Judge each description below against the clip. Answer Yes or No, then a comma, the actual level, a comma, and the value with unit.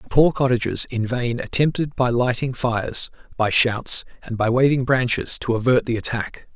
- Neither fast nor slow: Yes, average, 175 wpm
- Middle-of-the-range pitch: No, low, 125 Hz